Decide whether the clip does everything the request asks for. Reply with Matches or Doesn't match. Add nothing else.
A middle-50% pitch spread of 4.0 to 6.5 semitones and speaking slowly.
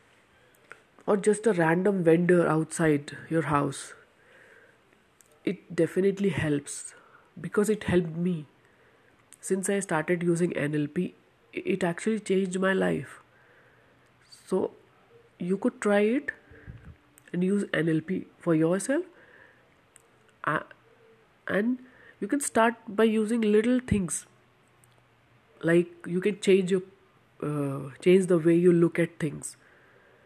Matches